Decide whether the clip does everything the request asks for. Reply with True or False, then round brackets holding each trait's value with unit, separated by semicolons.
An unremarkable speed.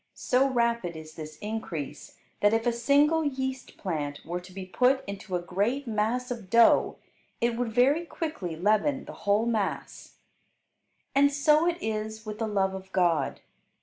True (165 wpm)